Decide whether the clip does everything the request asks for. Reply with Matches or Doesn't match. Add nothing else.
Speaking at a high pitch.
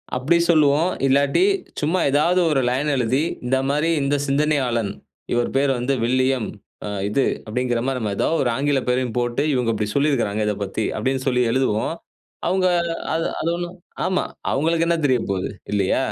Doesn't match